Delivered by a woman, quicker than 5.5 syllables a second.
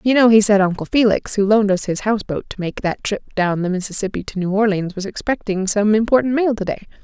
Yes: female; 6.1 syllables/s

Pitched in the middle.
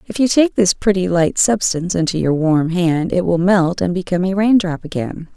Yes: medium, 180 Hz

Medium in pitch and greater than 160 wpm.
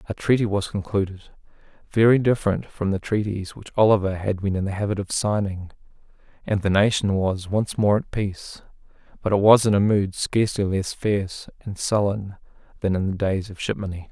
No: low, 100 Hz; average, 180 wpm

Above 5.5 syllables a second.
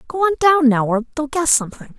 Yes: 6.3 syllables/s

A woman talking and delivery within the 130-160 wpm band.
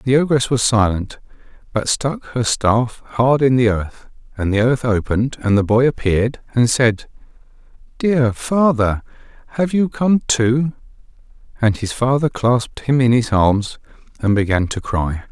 No: male; average, 155 wpm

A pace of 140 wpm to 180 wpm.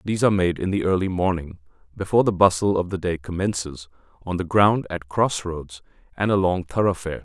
No: average, 190 wpm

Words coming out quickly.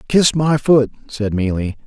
No: average, 160 wpm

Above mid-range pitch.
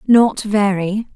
Yes: high, 205 Hz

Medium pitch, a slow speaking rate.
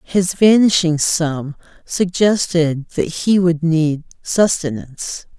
Yes: medium, 170 Hz; slow, 100 wpm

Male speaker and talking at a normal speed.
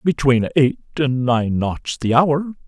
Yes: male; average, 155 wpm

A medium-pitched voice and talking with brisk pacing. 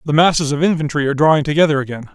Yes: medium, 150 Hz; fast, 225 wpm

